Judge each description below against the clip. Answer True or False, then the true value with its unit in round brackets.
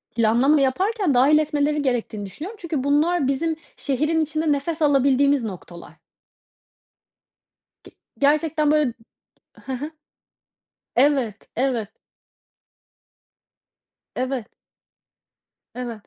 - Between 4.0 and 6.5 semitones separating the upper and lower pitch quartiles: False (3.5 semitones)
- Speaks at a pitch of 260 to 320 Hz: True (280 Hz)